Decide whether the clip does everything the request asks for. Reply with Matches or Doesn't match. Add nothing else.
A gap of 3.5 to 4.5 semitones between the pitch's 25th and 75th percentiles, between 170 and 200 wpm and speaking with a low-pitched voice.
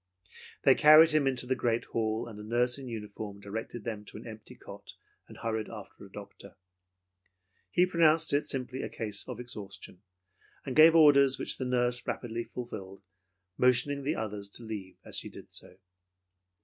Matches